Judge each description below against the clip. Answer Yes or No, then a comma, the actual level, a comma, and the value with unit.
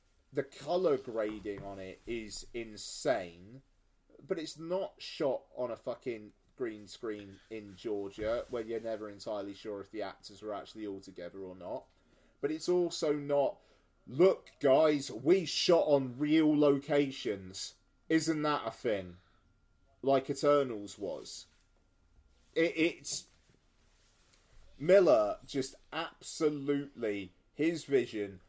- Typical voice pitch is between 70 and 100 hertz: No, low, 110 Hz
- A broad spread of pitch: Yes, wide, 7.0 semitones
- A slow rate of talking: Yes, slow, 120 wpm